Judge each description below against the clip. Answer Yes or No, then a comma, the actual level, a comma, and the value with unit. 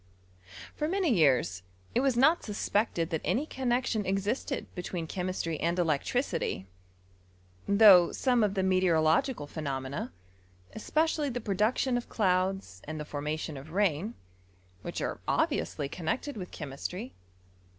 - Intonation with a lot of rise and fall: Yes, wide, 7.3 semitones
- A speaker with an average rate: No, slow, 130 wpm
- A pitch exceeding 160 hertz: Yes, high, 190 Hz